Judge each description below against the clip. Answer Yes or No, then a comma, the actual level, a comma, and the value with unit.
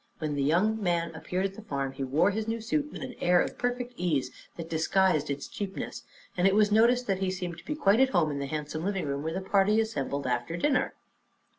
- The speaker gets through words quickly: Yes, fast, 230 wpm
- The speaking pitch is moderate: Yes, medium, 180 Hz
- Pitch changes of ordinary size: No, wide, 5.8 semitones